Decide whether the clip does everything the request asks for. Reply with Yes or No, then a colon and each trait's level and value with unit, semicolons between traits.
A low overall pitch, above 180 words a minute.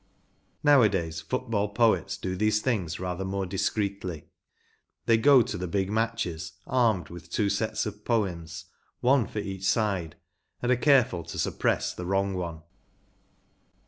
No: low, 100 Hz; average, 140 wpm